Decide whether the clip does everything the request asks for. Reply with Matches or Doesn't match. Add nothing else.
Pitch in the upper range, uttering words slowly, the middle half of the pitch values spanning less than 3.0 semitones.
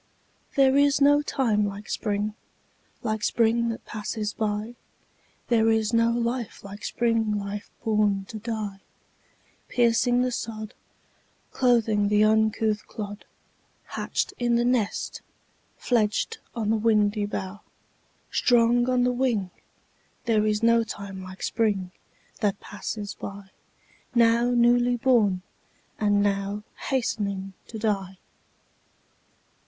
Matches